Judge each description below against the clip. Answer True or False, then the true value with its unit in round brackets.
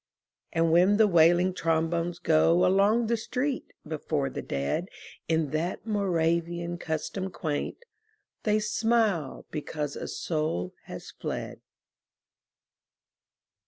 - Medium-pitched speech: True (170 Hz)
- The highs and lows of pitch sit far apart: False (4.0 semitones)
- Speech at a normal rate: False (105 wpm)